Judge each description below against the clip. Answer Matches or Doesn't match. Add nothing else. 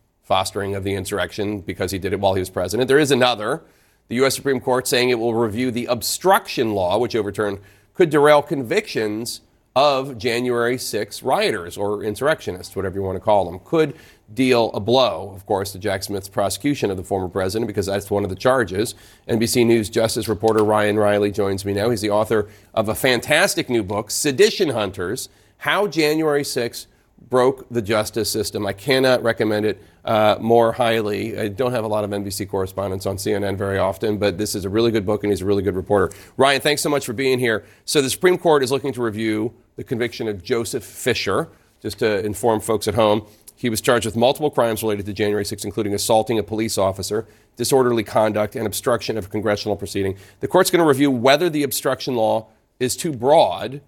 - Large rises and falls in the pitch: Doesn't match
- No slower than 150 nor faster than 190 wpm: Doesn't match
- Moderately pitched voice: Doesn't match